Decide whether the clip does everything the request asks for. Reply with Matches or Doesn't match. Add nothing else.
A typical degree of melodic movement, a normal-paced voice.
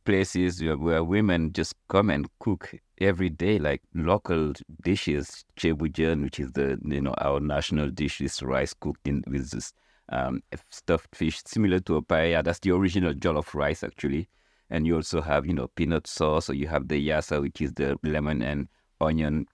Matches